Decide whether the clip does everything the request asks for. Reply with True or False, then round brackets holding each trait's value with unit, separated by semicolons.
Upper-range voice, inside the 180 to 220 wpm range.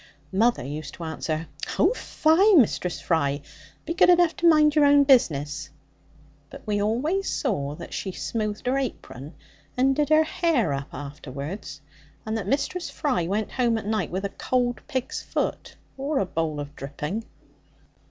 False (220 Hz; 160 wpm)